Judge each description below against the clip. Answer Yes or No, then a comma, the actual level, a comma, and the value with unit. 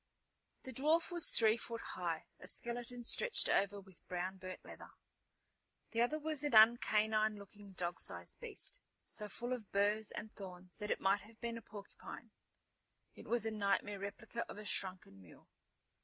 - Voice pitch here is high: Yes, high, 215 Hz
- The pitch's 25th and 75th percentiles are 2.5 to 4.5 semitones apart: Yes, average, 3.2 semitones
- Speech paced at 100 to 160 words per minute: No, average, 170 wpm